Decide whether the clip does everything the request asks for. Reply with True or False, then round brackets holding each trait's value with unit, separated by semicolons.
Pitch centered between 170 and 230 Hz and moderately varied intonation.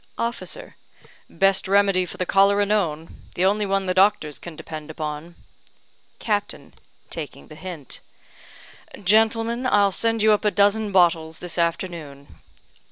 True (190 Hz; 3.8 semitones)